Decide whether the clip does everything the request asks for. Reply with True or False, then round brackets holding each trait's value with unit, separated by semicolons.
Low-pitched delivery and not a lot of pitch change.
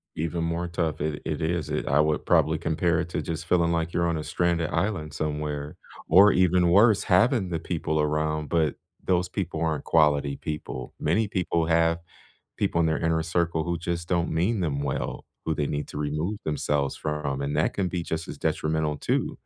True (80 Hz; 2.3 semitones)